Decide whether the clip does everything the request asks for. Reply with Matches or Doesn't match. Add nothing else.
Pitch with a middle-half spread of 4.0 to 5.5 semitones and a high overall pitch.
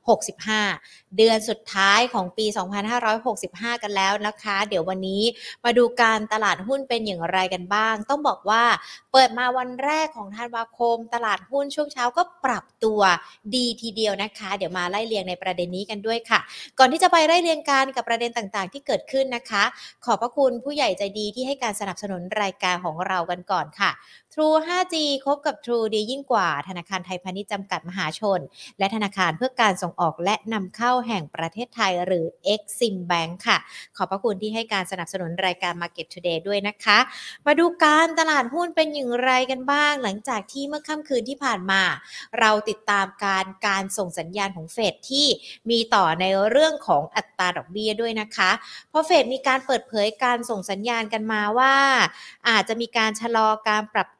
Matches